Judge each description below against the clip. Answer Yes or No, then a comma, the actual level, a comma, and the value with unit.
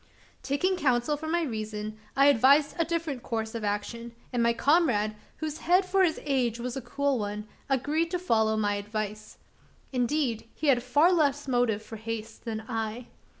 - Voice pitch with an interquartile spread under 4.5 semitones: No, average, 5.1 semitones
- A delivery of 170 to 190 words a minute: Yes, average, 175 wpm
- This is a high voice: Yes, high, 245 Hz